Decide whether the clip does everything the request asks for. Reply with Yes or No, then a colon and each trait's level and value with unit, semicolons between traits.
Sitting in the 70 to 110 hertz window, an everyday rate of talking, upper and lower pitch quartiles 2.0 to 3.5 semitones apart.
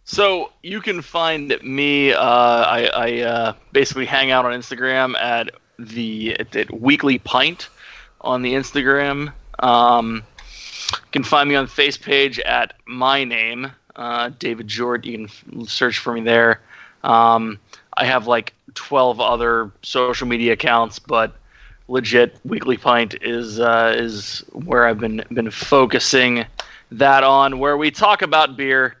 No: low, 125 Hz; average, 145 wpm; average, 2.9 semitones